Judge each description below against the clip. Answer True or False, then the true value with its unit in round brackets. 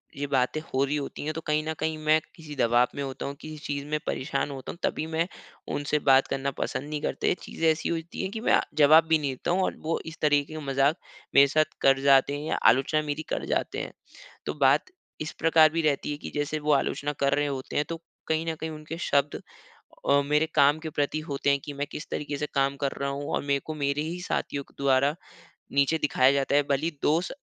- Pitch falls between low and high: True (145 Hz)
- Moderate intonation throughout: False (2.0 semitones)